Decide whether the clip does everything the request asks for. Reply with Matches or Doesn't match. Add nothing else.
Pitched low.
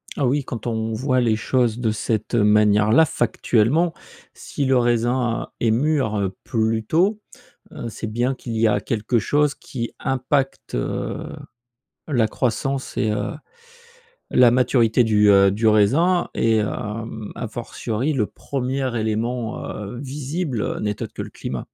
Matches